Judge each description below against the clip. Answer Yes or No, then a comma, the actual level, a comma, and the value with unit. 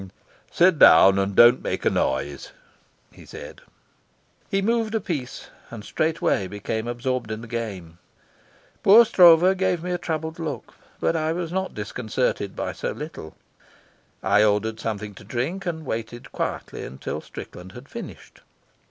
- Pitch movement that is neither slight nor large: No, wide, 8.1 semitones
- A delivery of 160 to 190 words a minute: No, average, 150 wpm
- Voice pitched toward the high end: No, low, 125 Hz